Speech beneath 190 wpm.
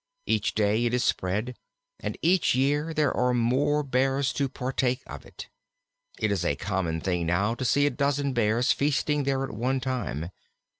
Yes: average, 180 wpm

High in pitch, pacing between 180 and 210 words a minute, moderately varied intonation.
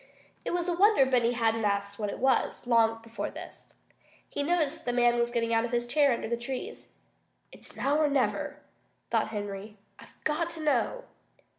Yes: high, 240 Hz; average, 190 wpm; average, 4.6 semitones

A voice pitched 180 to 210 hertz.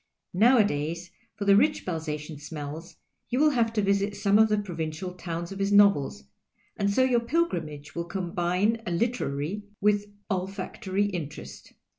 Yes: high, 190 Hz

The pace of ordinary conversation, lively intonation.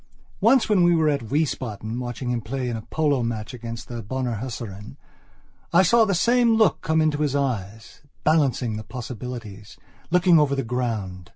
Yes: average, 175 wpm; wide, 5.9 semitones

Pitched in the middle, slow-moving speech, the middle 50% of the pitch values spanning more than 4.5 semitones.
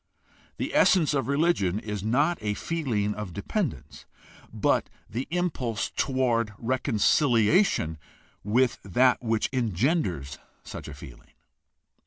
No: low, 120 Hz; slow, 110 wpm; average, 5.3 semitones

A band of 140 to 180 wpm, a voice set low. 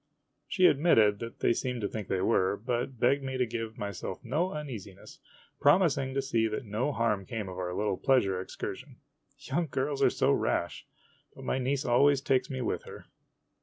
No: average, 190 wpm; low, 120 Hz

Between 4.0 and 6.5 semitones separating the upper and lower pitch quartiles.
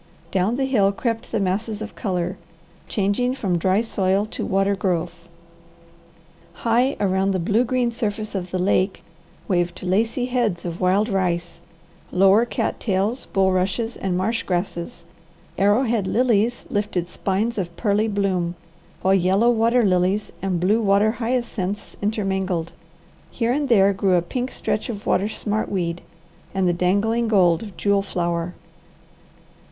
No: average, 3.5 semitones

